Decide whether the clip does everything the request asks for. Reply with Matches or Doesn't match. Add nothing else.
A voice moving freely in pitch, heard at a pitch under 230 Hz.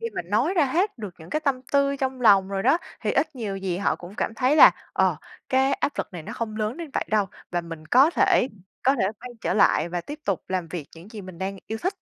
Matches